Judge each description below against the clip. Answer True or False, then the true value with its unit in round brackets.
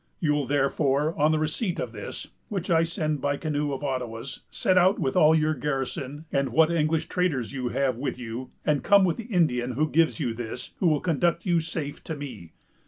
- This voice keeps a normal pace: False (210 wpm)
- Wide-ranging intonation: False (3.6 semitones)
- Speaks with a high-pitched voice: False (150 Hz)